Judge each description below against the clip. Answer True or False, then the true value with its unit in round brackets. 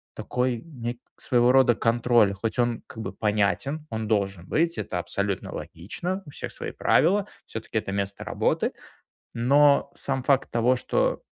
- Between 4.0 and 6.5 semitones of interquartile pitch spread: True (4.7 semitones)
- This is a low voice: True (120 Hz)